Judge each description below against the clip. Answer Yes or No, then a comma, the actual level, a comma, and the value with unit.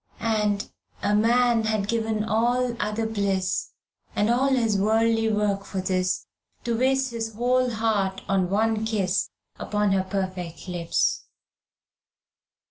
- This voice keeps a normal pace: No, slow, 125 wpm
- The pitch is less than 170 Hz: No, high, 215 Hz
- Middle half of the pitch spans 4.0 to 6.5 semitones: No, average, 2.7 semitones